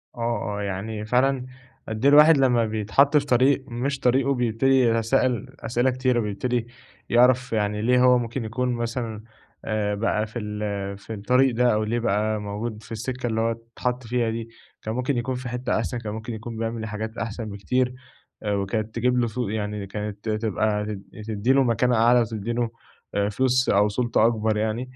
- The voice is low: Yes, low, 115 Hz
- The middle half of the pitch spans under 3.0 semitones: Yes, narrow, 2.6 semitones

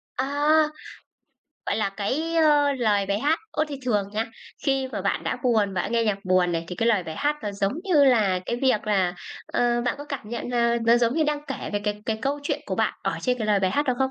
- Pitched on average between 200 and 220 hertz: No, high, 235 Hz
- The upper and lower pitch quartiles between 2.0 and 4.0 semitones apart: No, average, 4.8 semitones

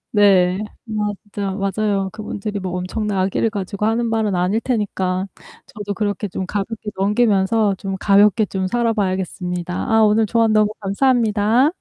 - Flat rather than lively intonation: Yes, narrow, 2.3 semitones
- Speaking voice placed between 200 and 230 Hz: Yes, high, 205 Hz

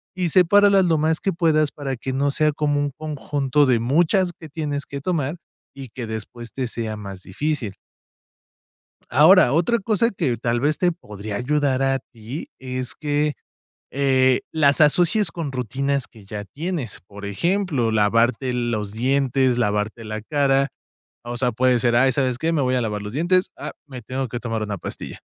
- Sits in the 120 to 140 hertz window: Yes, low, 135 Hz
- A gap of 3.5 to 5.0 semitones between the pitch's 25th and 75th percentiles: Yes, average, 4.5 semitones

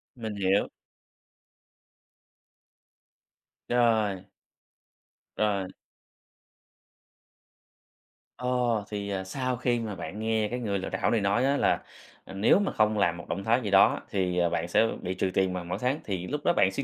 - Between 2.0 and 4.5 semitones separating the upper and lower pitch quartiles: Yes, average, 3.6 semitones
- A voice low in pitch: Yes, low, 100 Hz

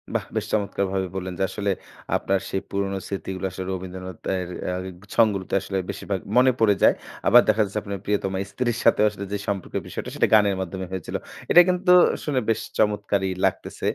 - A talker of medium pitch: No, low, 100 Hz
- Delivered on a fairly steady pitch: Yes, narrow, 2.0 semitones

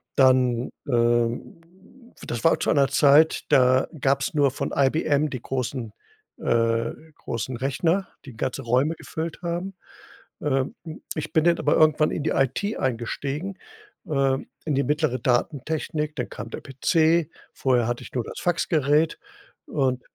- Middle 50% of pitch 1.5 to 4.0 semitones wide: Yes, average, 3.7 semitones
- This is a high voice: No, low, 135 Hz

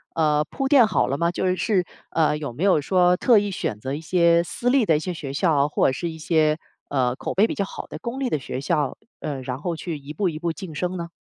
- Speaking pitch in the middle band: Yes, medium, 165 Hz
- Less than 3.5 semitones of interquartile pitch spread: No, average, 4.0 semitones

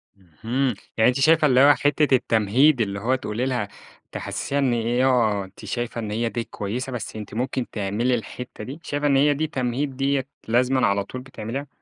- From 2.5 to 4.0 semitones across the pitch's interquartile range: Yes, average, 3.4 semitones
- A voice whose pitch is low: Yes, low, 125 Hz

